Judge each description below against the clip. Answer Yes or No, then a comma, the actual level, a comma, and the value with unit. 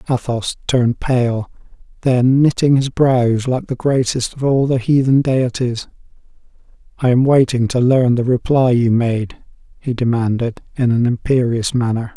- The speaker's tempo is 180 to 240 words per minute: No, average, 145 wpm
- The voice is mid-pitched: No, low, 125 Hz